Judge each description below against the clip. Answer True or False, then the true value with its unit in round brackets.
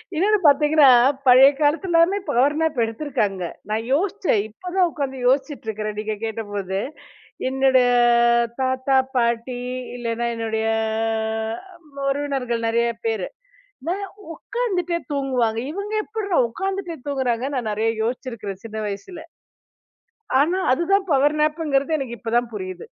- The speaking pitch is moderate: False (265 Hz)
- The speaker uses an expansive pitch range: True (5.8 semitones)